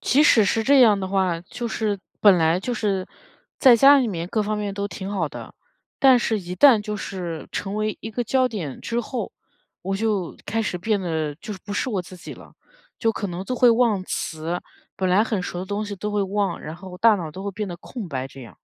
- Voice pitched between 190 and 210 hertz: Yes, high, 200 Hz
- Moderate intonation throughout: Yes, average, 3.6 semitones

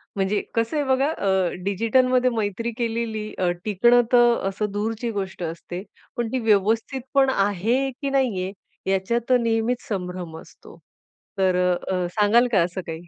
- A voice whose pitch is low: No, high, 215 Hz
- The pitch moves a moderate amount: Yes, average, 4.1 semitones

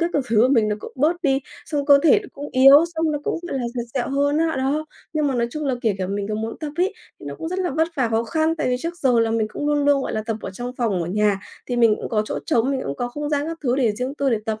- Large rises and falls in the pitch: No, average, 4.8 semitones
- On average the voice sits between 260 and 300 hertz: Yes, very high, 265 Hz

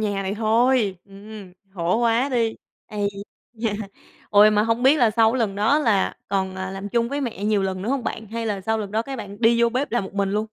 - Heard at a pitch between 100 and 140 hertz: No, high, 215 Hz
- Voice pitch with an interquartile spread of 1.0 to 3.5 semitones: Yes, average, 2.8 semitones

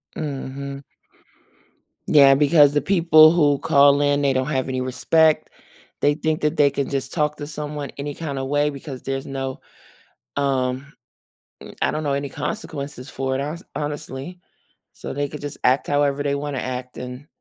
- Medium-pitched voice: Yes, medium, 145 Hz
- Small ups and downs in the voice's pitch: Yes, narrow, 1.8 semitones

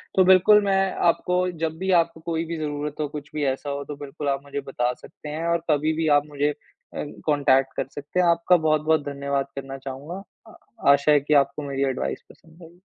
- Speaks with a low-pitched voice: No, medium, 150 Hz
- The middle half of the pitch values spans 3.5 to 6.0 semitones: No, average, 2.7 semitones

